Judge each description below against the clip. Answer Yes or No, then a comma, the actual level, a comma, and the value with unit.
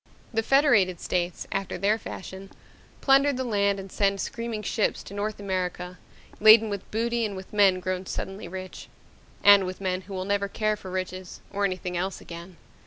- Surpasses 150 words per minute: Yes, average, 175 wpm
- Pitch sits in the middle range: No, high, 195 Hz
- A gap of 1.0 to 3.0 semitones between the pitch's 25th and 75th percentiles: Yes, narrow, 2.4 semitones